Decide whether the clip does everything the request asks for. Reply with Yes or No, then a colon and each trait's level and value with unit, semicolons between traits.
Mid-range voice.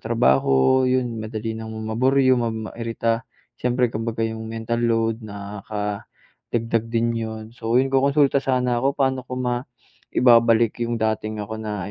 No: low, 115 Hz